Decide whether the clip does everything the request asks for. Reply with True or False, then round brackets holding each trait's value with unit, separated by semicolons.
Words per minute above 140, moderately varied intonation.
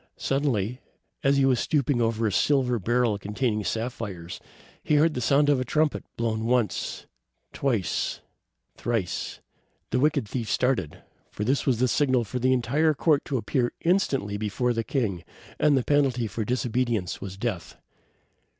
True (155 wpm; 3.8 semitones)